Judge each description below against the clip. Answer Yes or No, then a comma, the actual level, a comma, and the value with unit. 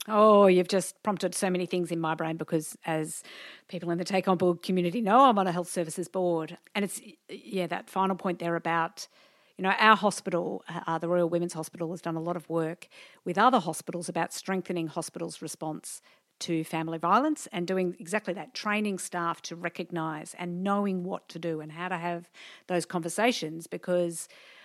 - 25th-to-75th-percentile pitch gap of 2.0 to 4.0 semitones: Yes, narrow, 2.4 semitones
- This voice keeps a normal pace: Yes, average, 190 wpm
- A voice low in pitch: No, medium, 175 Hz